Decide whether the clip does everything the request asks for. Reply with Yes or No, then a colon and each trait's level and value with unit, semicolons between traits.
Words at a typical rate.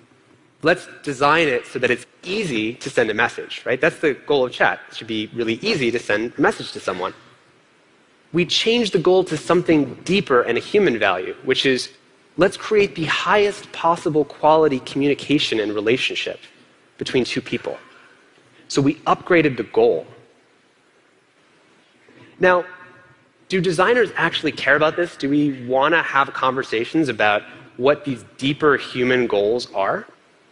Yes: average, 155 wpm